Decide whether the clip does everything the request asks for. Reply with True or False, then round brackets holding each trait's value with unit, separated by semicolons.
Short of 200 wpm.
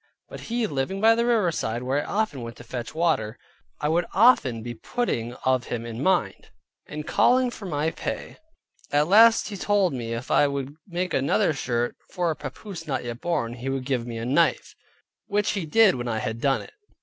False (205 wpm)